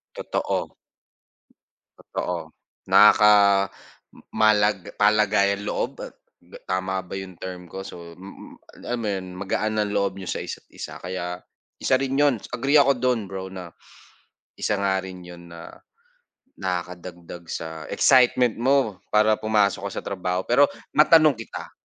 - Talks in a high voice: No, low, 100 Hz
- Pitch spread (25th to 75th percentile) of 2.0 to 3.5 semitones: Yes, average, 2.9 semitones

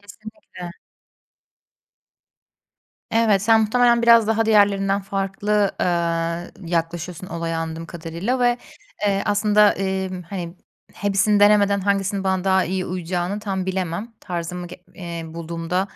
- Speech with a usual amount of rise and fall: Yes, average, 3.1 semitones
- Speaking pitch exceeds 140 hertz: Yes, high, 190 Hz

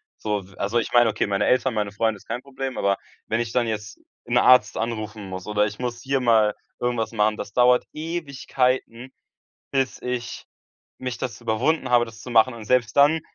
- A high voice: No, low, 120 Hz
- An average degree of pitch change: Yes, average, 3.0 semitones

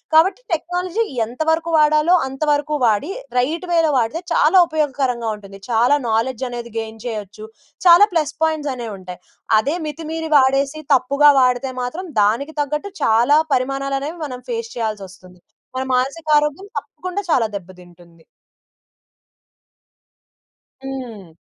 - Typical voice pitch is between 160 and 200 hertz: No, very high, 270 Hz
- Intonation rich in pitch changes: Yes, wide, 5.8 semitones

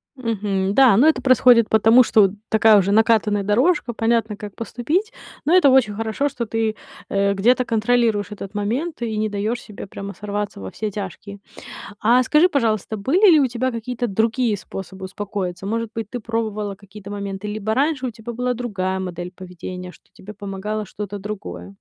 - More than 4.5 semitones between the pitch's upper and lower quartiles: No, average, 3.2 semitones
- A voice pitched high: Yes, high, 215 Hz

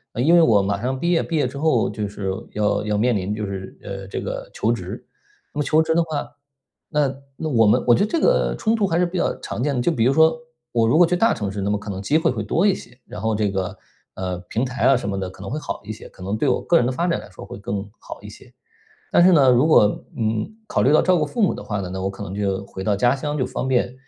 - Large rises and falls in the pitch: Yes, wide, 7.8 semitones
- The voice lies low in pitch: Yes, low, 120 Hz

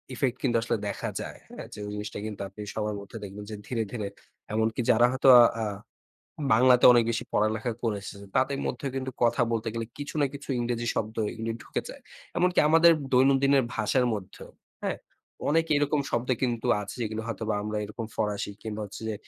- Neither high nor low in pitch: No, low, 115 Hz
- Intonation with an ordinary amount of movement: Yes, average, 3.2 semitones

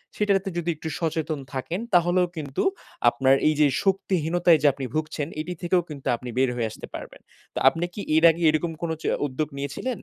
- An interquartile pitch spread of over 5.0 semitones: No, average, 3.7 semitones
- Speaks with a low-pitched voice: No, medium, 160 Hz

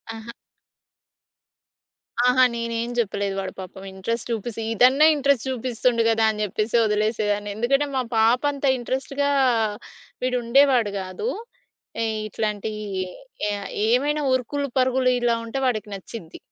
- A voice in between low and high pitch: No, high, 230 Hz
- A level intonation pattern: No, average, 3.3 semitones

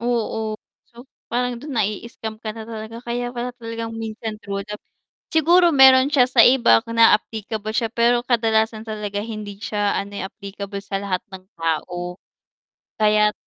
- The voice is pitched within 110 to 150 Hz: No, high, 220 Hz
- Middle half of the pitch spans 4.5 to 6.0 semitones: No, narrow, 2.4 semitones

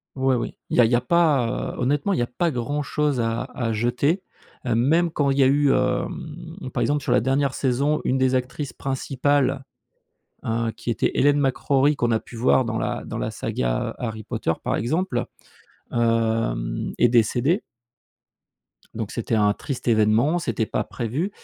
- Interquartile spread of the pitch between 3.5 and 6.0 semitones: Yes, average, 3.8 semitones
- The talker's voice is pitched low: Yes, low, 130 Hz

